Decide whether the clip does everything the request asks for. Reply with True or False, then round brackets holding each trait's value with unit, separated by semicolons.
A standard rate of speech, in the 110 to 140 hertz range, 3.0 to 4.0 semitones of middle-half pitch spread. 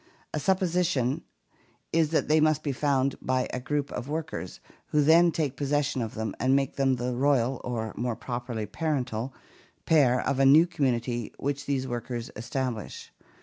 True (165 wpm; 135 Hz; 3.5 semitones)